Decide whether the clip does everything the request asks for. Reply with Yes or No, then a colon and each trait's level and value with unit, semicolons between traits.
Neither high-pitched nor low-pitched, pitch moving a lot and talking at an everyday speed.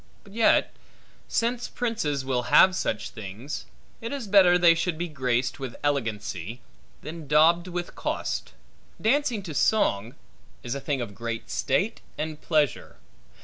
Yes: medium, 150 Hz; wide, 7.0 semitones; average, 145 wpm